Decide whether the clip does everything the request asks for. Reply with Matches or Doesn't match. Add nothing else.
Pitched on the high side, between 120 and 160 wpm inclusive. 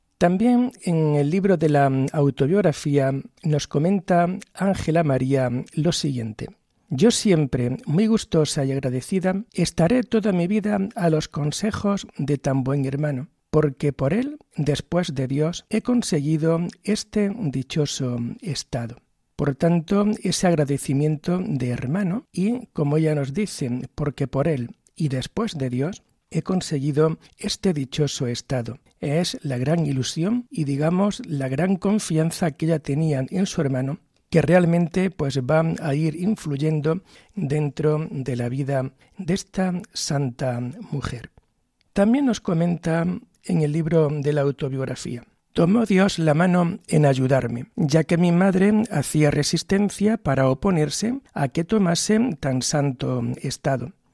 Doesn't match